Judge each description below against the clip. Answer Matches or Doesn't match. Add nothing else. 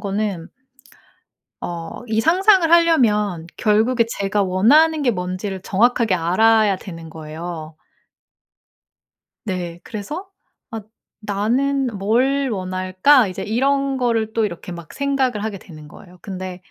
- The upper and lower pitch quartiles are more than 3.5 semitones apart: Matches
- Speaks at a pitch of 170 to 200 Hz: Doesn't match